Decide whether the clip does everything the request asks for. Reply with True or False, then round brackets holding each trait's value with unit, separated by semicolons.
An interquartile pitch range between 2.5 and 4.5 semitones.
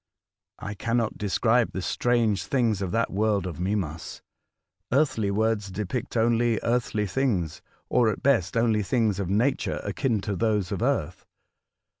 True (3.1 semitones)